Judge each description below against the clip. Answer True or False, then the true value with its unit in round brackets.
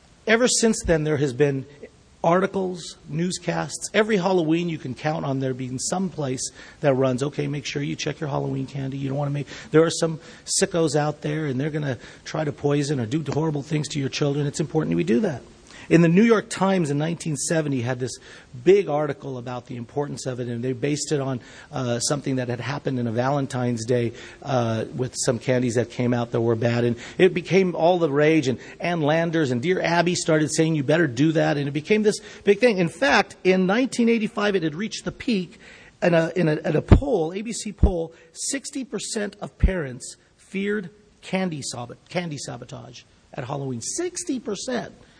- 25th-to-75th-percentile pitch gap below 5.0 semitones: False (5.3 semitones)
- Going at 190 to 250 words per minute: True (200 wpm)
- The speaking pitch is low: False (155 Hz)